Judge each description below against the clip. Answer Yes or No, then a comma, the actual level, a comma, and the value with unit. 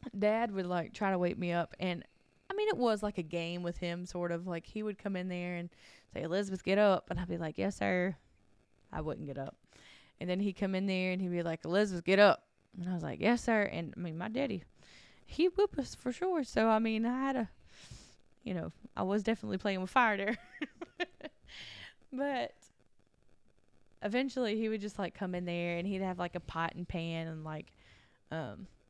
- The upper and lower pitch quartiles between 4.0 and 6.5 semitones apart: Yes, average, 4.3 semitones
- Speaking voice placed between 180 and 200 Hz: Yes, high, 190 Hz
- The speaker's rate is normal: No, fast, 220 wpm